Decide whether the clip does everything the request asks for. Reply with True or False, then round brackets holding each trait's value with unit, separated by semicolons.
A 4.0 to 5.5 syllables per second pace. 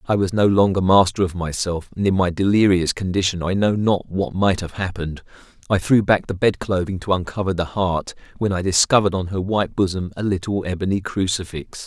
False (5.7 syllables/s)